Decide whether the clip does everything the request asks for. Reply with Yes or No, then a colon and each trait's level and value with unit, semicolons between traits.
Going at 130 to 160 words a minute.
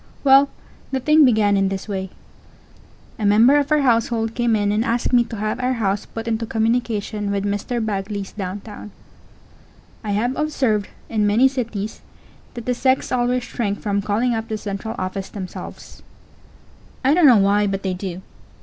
No: average, 170 wpm